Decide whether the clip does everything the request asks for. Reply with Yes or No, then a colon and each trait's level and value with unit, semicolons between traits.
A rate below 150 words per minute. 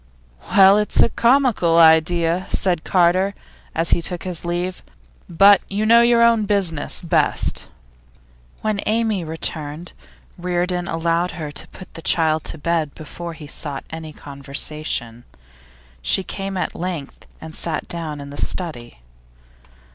Yes: average, 140 wpm